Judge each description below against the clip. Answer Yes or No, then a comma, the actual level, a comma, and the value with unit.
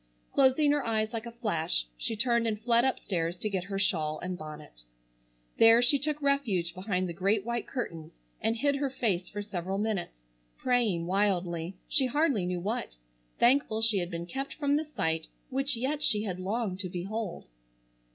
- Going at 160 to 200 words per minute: Yes, average, 180 wpm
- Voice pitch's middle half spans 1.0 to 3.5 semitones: No, wide, 5.6 semitones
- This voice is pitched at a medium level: No, high, 210 Hz